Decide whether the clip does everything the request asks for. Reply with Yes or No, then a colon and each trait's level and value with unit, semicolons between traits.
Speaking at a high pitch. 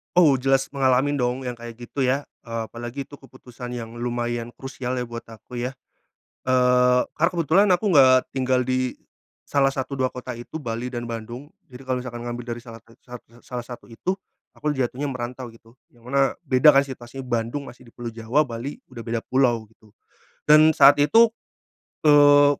No: low, 125 Hz